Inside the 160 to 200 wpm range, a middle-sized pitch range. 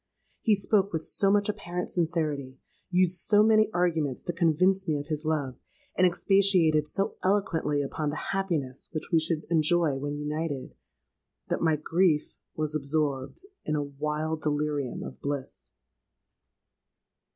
No: average, 140 wpm; average, 3.6 semitones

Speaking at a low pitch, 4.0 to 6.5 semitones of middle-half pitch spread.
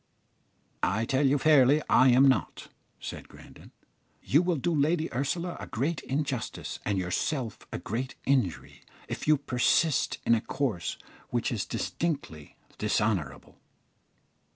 Yes: low, 130 Hz; average, 5.2 semitones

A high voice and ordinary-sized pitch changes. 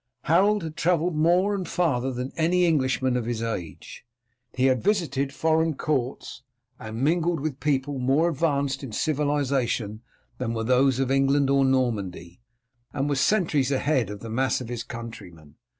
No: low, 135 Hz; average, 4.3 semitones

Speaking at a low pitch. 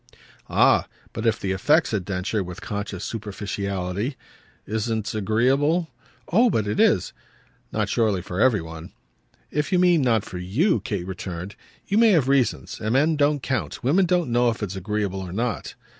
Yes: low, 110 Hz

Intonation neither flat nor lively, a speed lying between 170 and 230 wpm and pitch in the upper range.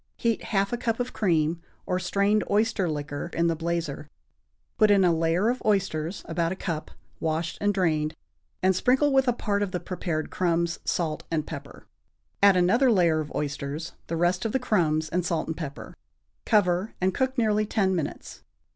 No: average, 4.2 semitones; average, 180 wpm; medium, 180 Hz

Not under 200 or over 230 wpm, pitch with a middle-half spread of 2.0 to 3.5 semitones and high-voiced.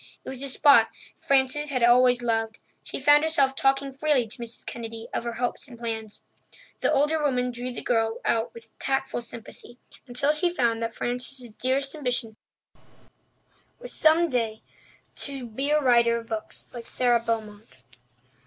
No: average, 160 wpm; average, 3.0 semitones; high, 245 Hz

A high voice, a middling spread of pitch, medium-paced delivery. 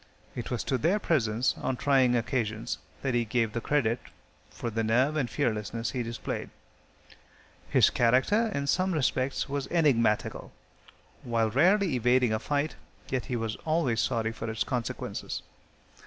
No: low, 125 Hz; average, 3.8 semitones; average, 150 wpm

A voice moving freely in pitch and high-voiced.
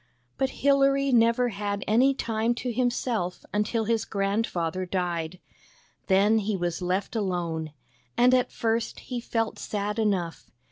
No: average, 4.3 semitones; high, 215 Hz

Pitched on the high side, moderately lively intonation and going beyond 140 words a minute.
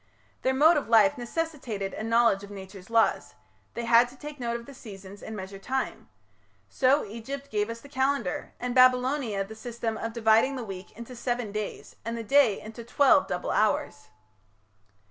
Yes: high, 235 Hz; average, 3.7 semitones; average, 180 wpm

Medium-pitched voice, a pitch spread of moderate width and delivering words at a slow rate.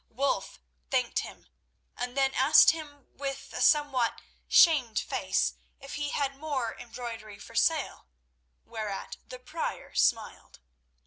No: very high, 270 Hz; average, 3.6 semitones; slow, 125 wpm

